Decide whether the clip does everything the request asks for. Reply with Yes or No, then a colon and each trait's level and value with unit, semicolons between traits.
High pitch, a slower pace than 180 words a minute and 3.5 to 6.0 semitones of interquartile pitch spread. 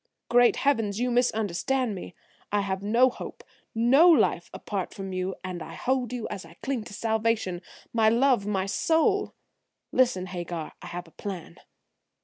Yes: high, 220 Hz; average, 160 wpm; average, 4.7 semitones